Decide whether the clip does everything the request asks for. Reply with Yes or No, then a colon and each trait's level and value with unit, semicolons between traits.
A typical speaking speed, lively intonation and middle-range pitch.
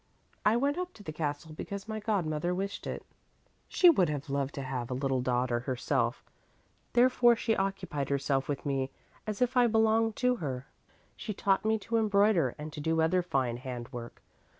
Yes: average, 180 wpm; wide, 8.2 semitones; medium, 160 Hz